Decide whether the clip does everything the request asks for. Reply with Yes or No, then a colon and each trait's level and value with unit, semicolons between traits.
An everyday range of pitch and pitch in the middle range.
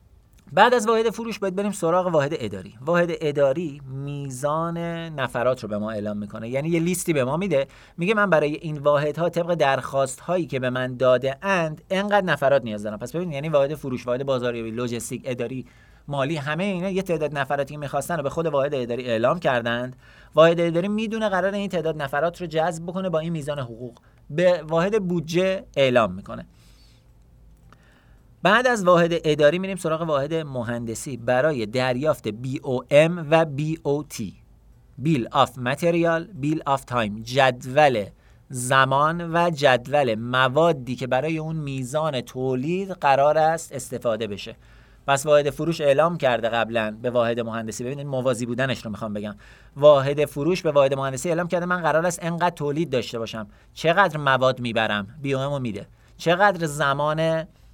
Yes: average, 5.0 semitones; medium, 145 Hz